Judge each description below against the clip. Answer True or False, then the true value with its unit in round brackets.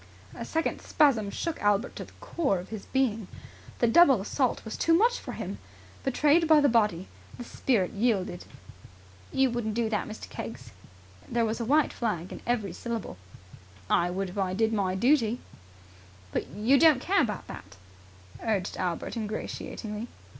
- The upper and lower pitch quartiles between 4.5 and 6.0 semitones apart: True (5.2 semitones)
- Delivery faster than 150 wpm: True (165 wpm)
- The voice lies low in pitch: False (225 Hz)